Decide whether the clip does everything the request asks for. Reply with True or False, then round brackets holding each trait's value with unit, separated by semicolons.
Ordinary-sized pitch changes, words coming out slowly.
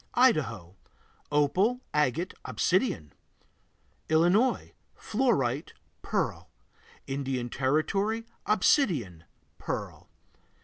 False (8.5 semitones; 60 wpm)